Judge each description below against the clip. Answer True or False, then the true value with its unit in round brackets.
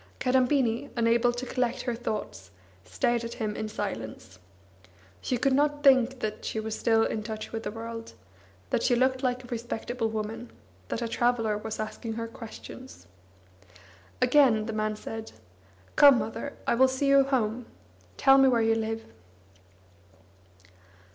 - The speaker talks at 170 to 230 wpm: False (155 wpm)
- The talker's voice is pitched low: False (230 Hz)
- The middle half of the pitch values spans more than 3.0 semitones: False (2.6 semitones)